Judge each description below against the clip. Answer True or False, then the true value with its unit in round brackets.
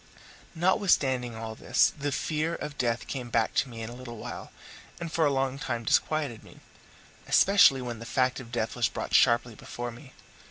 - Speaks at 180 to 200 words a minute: True (190 wpm)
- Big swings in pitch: False (3.6 semitones)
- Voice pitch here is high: False (125 Hz)